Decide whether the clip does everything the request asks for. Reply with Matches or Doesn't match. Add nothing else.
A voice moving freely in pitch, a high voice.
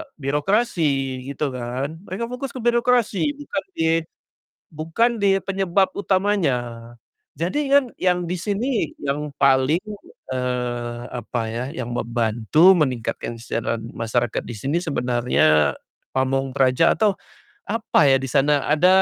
Doesn't match